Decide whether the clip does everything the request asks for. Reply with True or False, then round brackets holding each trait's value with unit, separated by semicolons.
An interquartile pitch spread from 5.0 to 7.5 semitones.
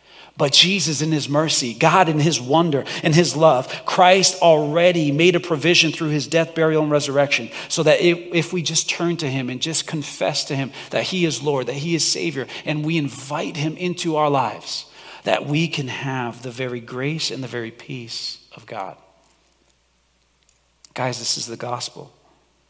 False (4.1 semitones)